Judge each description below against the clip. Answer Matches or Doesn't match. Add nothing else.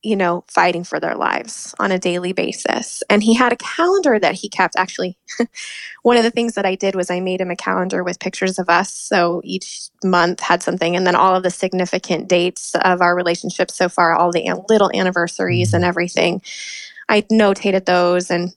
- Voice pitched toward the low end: Doesn't match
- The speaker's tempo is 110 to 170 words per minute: Doesn't match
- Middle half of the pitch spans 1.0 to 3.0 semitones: Matches